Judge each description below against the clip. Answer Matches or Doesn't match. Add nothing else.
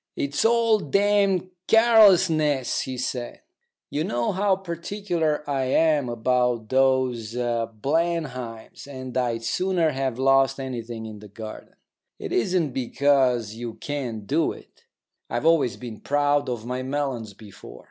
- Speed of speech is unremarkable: Doesn't match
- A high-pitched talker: Doesn't match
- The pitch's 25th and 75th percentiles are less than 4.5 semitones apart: Doesn't match